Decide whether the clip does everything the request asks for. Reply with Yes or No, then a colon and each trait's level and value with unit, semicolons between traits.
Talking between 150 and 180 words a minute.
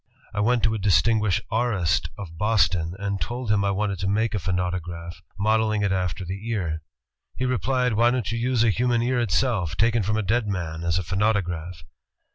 No: average, 195 wpm